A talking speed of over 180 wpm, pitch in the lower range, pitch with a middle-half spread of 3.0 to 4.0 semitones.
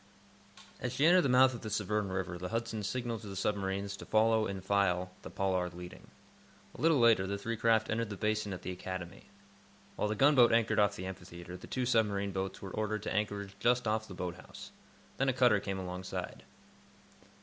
Yes: fast, 205 wpm; low, 105 Hz; average, 3.4 semitones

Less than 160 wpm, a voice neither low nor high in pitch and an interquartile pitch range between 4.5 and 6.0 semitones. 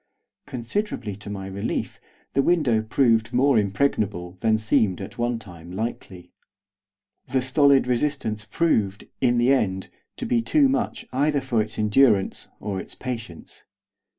No: average, 140 wpm; low, 115 Hz; average, 5.0 semitones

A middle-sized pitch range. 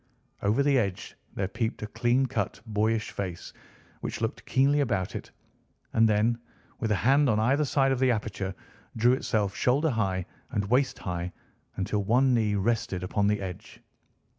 Yes: average, 4.1 semitones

